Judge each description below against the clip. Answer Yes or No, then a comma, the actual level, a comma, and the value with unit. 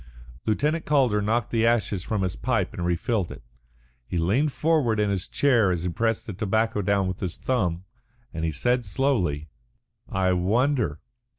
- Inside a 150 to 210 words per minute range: Yes, average, 170 wpm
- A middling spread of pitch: Yes, average, 5.0 semitones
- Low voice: Yes, low, 105 Hz